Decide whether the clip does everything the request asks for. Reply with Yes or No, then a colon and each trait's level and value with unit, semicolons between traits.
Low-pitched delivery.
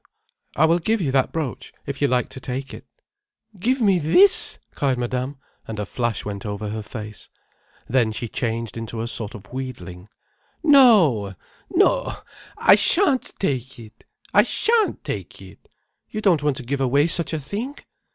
Yes: low, 130 Hz